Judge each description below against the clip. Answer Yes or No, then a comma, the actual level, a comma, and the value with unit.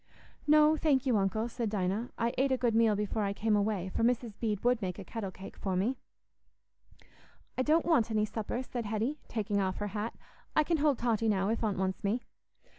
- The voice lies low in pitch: No, high, 220 Hz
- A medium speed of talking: No, fast, 210 wpm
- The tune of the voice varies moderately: Yes, average, 3.4 semitones